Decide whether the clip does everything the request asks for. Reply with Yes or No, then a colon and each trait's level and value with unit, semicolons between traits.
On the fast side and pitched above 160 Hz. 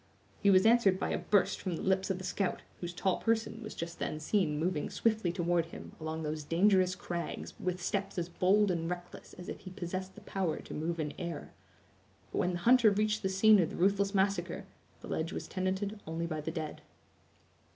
Yes: fast, 210 wpm; medium, 185 Hz